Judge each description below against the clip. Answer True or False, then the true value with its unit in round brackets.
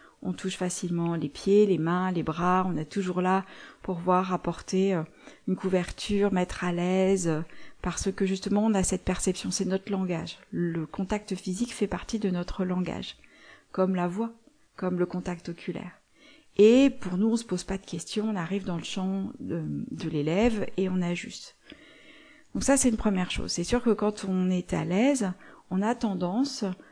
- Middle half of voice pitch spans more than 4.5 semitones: False (2.4 semitones)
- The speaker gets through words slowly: False (185 wpm)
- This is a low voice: False (190 Hz)